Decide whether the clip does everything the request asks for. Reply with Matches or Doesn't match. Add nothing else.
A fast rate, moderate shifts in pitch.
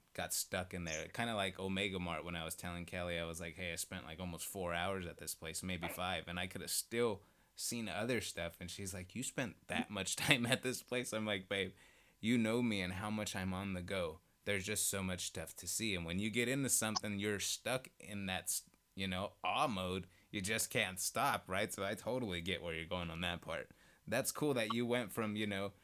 Matches